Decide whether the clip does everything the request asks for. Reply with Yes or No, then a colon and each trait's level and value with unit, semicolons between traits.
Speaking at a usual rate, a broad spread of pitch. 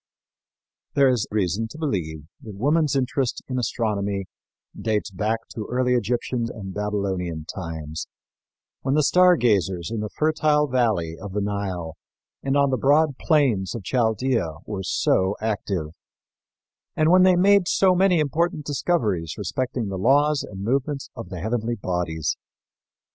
Yes: average, 145 wpm; wide, 6.4 semitones